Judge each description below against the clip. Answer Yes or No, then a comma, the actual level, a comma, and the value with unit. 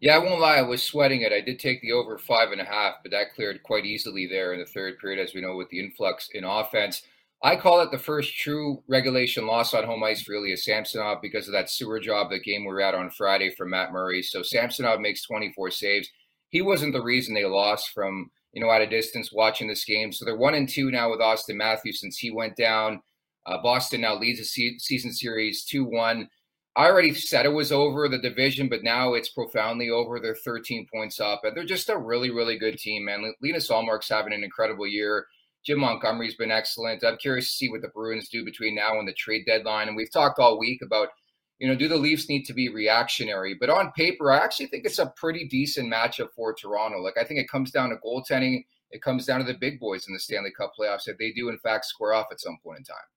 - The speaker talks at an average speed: No, fast, 245 wpm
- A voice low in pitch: Yes, low, 115 Hz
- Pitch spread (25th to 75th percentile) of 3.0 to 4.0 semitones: Yes, average, 3.5 semitones